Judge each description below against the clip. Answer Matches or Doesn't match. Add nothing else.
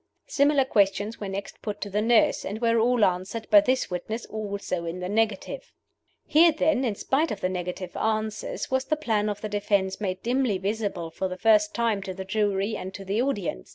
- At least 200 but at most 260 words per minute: Matches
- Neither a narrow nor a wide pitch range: Matches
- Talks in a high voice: Matches